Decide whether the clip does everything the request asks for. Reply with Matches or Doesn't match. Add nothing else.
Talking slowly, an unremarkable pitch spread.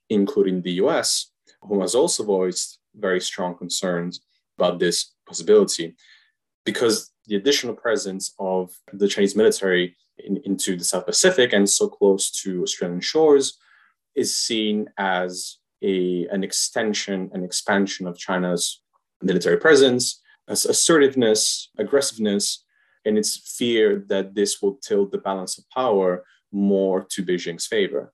Doesn't match